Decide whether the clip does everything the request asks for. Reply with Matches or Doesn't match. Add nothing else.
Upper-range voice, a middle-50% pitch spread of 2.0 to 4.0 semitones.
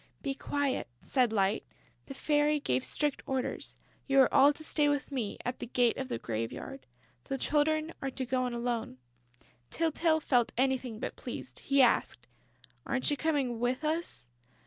Matches